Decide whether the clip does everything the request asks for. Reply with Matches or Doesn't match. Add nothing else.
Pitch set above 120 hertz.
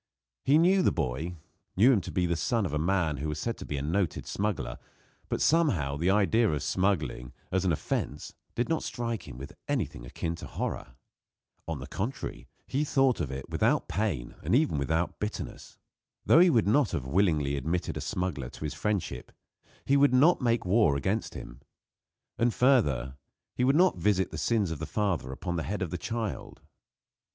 Doesn't match